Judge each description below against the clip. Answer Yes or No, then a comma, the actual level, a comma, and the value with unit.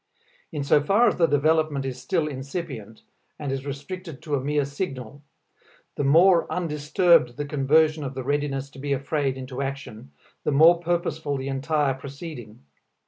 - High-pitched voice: No, medium, 145 Hz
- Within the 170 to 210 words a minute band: No, average, 160 wpm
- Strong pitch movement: No, average, 2.9 semitones